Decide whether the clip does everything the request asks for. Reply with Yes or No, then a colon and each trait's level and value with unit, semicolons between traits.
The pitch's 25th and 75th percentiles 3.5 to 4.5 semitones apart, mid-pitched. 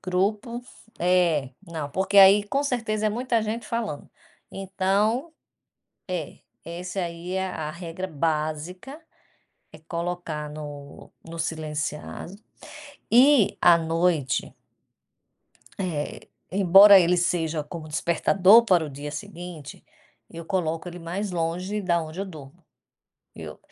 Yes: average, 3.8 semitones; medium, 175 Hz